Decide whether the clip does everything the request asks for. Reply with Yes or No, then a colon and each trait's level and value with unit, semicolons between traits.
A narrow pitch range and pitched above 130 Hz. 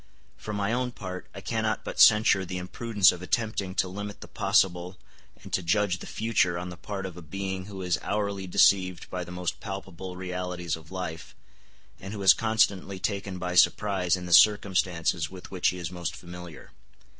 No: narrow, 2.1 semitones; very low, 95 Hz